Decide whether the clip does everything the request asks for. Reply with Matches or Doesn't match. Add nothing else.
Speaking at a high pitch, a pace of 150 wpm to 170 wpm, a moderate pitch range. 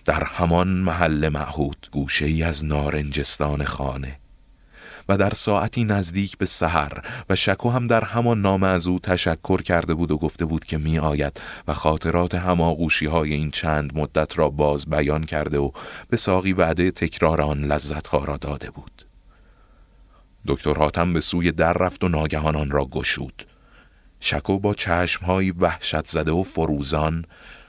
Doesn't match